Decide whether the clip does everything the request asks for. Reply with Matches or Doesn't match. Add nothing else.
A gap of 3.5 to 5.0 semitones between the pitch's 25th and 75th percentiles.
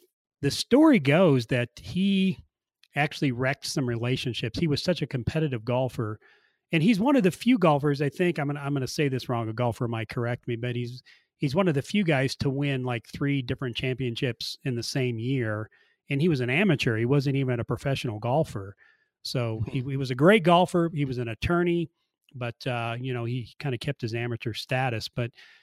Matches